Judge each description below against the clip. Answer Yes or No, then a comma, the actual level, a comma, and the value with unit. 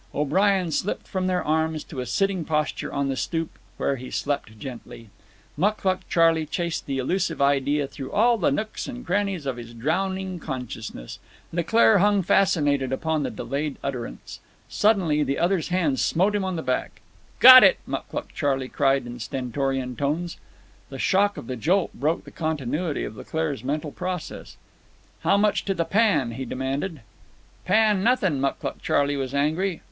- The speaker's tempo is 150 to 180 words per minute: Yes, average, 160 wpm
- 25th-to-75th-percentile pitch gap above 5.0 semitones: Yes, wide, 5.6 semitones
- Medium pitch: Yes, medium, 155 Hz